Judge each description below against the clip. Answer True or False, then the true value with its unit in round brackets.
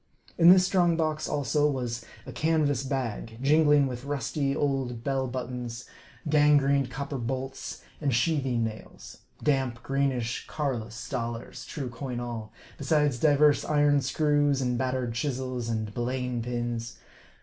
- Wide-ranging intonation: False (3.3 semitones)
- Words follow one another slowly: True (130 wpm)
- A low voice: True (130 Hz)